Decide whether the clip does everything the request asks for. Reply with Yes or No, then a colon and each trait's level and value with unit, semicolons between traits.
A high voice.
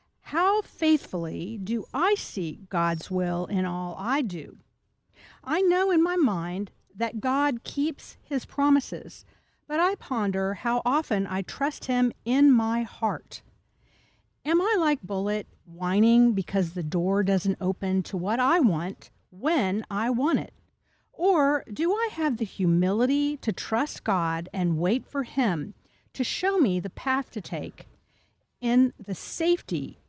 Yes: high, 235 Hz